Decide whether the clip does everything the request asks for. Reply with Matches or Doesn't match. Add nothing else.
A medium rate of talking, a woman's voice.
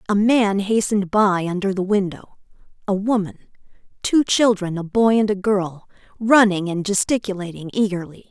Matches